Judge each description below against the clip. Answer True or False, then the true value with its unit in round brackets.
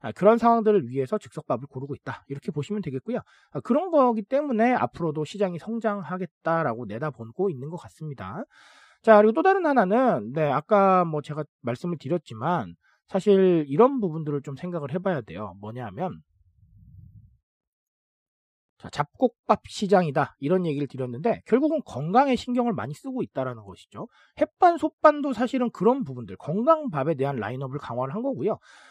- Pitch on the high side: False (175 Hz)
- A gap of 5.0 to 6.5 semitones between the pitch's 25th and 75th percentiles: False (8.7 semitones)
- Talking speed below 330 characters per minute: False (350 characters per minute)